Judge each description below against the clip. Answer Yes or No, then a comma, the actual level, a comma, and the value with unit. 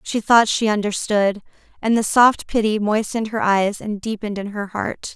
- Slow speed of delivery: No, average, 185 wpm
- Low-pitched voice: No, high, 210 Hz